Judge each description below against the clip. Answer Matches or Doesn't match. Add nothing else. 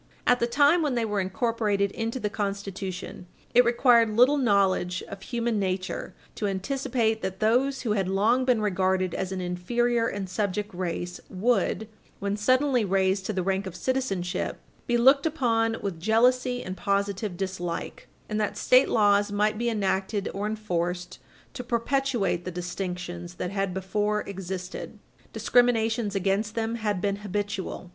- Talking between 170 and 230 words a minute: Doesn't match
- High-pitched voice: Matches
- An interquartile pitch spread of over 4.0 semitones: Doesn't match